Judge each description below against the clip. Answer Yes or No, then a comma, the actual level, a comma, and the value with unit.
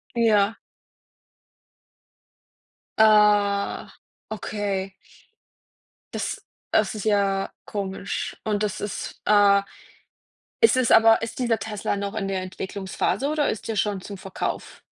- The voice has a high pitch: Yes, high, 205 Hz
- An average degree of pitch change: No, narrow, 1.7 semitones